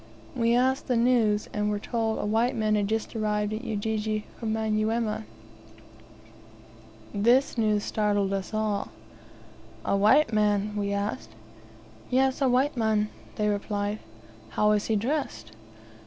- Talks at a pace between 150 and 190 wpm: No, average, 140 wpm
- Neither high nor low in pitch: No, high, 215 Hz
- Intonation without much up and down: Yes, narrow, 1.8 semitones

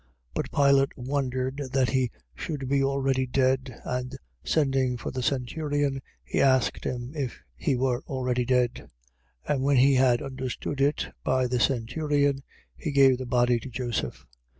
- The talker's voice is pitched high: No, low, 130 Hz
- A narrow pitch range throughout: Yes, narrow, 1.6 semitones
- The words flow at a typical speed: Yes, average, 160 wpm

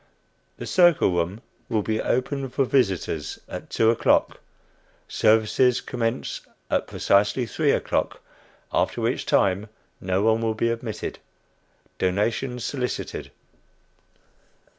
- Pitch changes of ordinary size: Yes, average, 3.6 semitones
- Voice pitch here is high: No, low, 115 Hz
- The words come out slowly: Yes, slow, 110 wpm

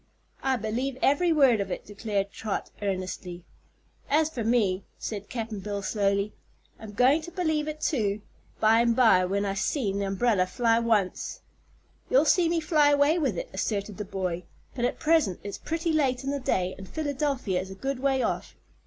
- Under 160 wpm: No, average, 180 wpm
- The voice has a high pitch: Yes, high, 225 Hz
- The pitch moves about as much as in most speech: No, wide, 6.2 semitones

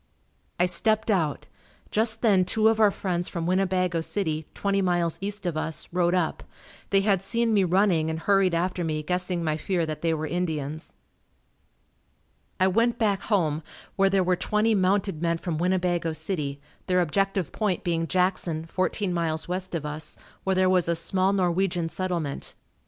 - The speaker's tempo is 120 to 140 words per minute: No, average, 170 wpm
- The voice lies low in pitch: No, medium, 180 Hz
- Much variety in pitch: No, average, 2.9 semitones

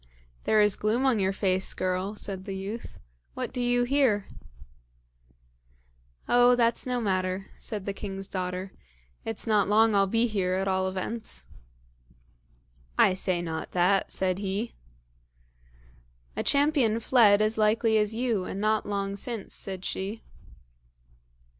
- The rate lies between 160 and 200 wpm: No, average, 140 wpm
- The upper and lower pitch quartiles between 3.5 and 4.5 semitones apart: No, average, 3.1 semitones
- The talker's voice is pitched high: Yes, high, 205 Hz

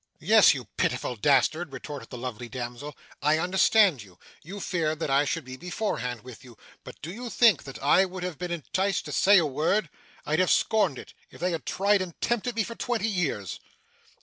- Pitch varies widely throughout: Yes, wide, 6.1 semitones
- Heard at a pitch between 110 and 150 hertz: No, medium, 165 Hz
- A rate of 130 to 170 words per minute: No, average, 200 wpm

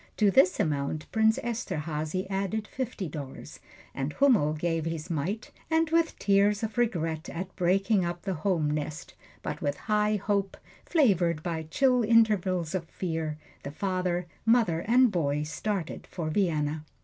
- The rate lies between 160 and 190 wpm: No, average, 150 wpm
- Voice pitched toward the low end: No, medium, 185 Hz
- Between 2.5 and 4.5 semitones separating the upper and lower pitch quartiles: No, average, 5.0 semitones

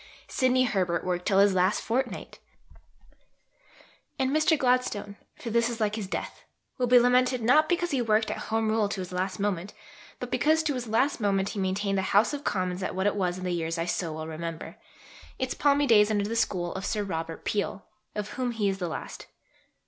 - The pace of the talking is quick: Yes, fast, 210 wpm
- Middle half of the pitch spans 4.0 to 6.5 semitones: Yes, average, 5.0 semitones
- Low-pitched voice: No, high, 210 Hz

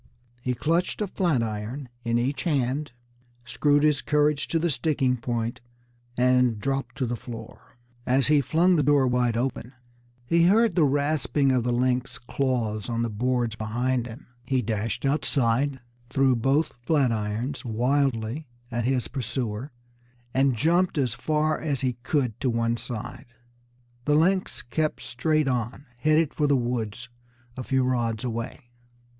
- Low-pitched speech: Yes, low, 130 Hz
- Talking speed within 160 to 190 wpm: No, average, 150 wpm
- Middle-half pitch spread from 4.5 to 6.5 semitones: No, average, 3.6 semitones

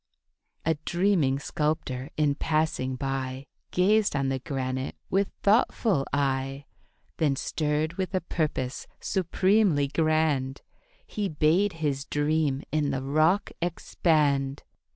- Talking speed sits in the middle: No, slow, 110 wpm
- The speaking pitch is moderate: Yes, medium, 150 Hz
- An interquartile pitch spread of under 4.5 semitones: Yes, average, 3.8 semitones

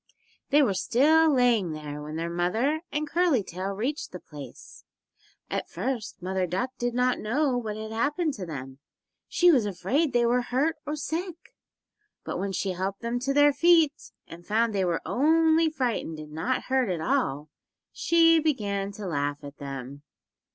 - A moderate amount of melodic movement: No, wide, 8.4 semitones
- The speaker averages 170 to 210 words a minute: Yes, average, 175 wpm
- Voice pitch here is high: Yes, high, 230 Hz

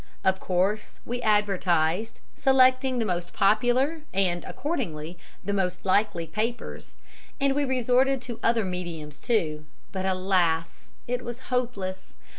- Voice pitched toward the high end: Yes, high, 205 Hz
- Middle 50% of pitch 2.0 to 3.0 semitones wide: No, wide, 5.4 semitones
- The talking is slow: Yes, slow, 125 wpm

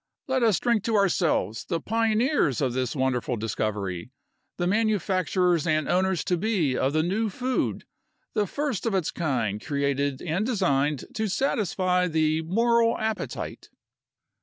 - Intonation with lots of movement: Yes, wide, 7.5 semitones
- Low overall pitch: No, medium, 180 Hz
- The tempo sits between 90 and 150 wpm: Yes, average, 140 wpm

